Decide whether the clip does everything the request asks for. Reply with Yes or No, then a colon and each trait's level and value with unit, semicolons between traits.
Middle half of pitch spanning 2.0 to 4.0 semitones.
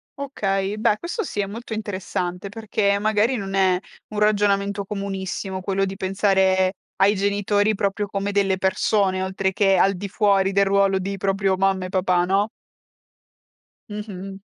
No: narrow, 1.3 semitones